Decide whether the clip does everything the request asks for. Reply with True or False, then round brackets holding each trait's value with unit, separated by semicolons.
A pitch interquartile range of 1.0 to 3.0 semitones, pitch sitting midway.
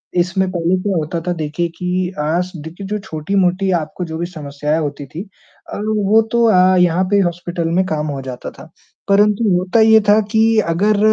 False (3.7 semitones; 180 Hz)